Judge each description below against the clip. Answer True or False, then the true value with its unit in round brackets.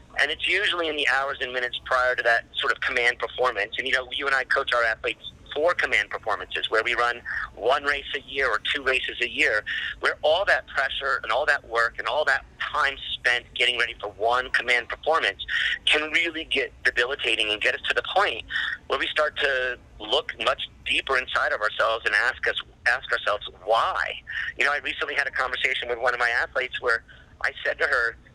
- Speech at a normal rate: False (215 wpm)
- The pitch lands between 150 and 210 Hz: False (125 Hz)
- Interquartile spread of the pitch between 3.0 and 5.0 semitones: False (2.6 semitones)